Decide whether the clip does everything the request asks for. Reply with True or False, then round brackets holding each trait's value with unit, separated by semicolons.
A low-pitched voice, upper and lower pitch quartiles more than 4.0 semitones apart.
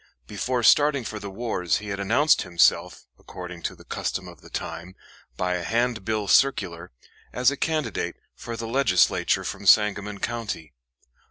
True (105 Hz; 4.7 semitones)